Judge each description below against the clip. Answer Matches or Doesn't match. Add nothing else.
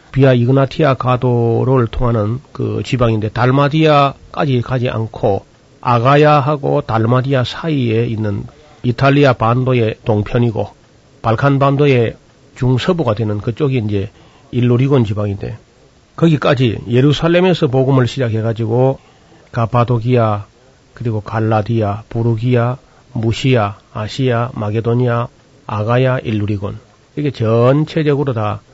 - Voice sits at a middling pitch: Doesn't match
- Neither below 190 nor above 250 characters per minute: Doesn't match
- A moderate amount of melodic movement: Matches